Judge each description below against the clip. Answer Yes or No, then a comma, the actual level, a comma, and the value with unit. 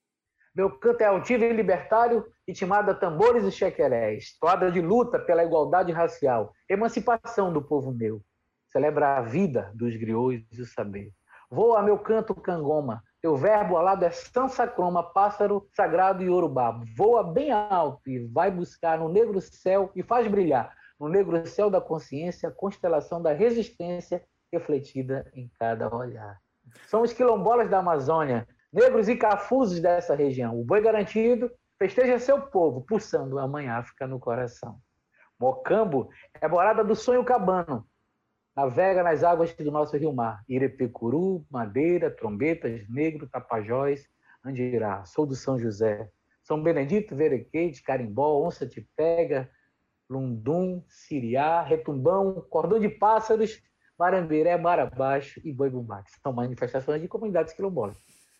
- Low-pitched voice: No, medium, 165 Hz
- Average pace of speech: Yes, average, 140 wpm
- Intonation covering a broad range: Yes, wide, 7.6 semitones